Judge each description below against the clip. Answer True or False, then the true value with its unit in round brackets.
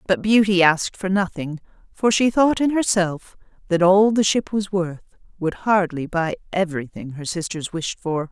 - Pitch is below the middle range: False (185 Hz)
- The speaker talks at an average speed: True (175 wpm)